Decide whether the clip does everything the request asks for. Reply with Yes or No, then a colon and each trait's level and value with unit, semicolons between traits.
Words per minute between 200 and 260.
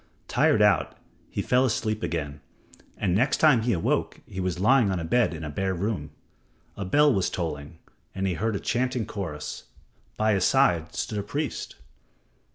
No: average, 175 wpm